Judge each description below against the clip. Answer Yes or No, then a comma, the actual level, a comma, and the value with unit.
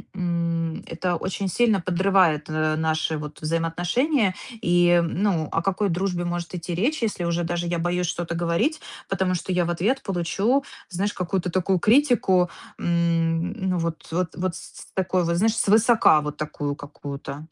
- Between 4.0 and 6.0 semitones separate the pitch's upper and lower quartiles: No, narrow, 2.6 semitones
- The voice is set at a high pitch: No, medium, 175 Hz